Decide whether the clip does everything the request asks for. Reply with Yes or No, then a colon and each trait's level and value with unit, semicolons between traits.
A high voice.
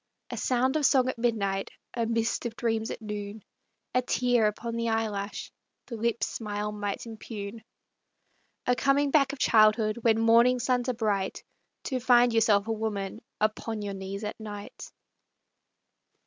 Yes: high, 225 Hz